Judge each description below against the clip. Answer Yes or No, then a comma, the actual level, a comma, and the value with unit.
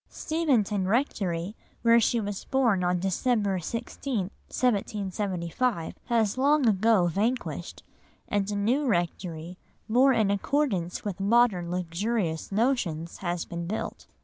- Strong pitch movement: No, average, 4.8 semitones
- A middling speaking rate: No, slow, 120 wpm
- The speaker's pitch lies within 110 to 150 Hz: No, high, 205 Hz